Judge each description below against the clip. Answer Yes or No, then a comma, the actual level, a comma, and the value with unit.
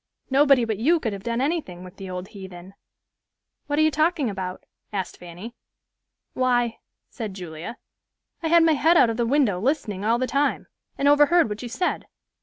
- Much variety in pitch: Yes, wide, 7.1 semitones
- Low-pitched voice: No, high, 235 Hz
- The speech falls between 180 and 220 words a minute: Yes, average, 185 wpm